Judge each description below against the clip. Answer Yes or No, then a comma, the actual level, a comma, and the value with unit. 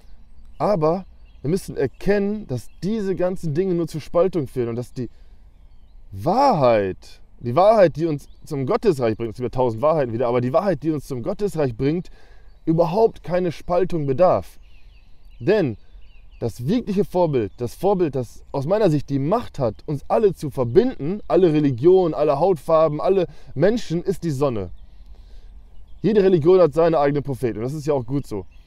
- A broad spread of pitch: Yes, wide, 7.3 semitones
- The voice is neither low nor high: Yes, medium, 145 Hz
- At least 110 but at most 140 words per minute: No, average, 165 wpm